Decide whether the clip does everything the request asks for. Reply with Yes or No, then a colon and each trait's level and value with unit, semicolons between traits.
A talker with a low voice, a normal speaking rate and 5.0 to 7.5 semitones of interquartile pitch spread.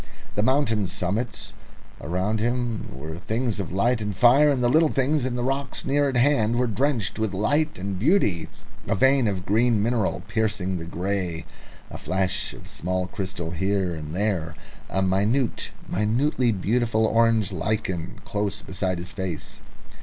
No: low, 105 Hz; average, 155 wpm; average, 4.6 semitones